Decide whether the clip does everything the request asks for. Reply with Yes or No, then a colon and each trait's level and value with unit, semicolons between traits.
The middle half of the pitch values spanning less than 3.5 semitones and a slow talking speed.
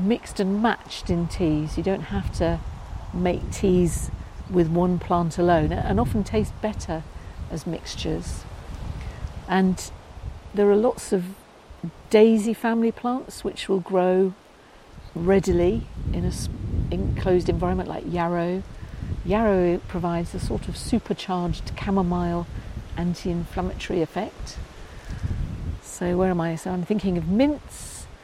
Yes: narrow, 2.6 semitones; slow, 125 wpm